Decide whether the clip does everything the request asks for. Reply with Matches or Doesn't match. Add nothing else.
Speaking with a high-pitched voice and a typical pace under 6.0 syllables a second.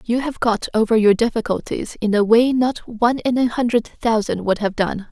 Matches